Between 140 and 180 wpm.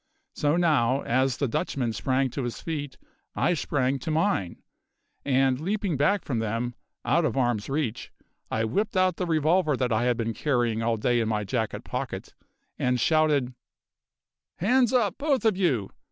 Yes: average, 170 wpm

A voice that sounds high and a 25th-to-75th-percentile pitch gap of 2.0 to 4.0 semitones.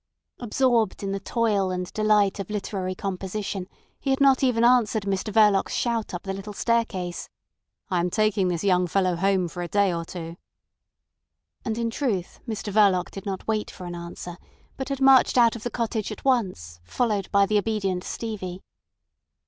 Yes: high, 200 Hz; average, 3.5 semitones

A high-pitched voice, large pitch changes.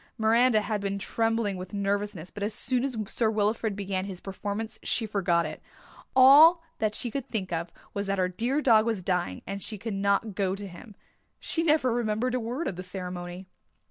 No: high, 205 Hz; average, 3.3 semitones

